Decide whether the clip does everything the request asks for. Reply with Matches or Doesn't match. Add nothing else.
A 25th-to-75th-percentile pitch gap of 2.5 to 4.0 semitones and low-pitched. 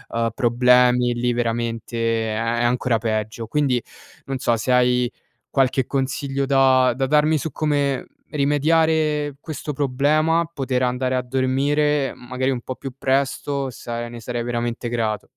Matches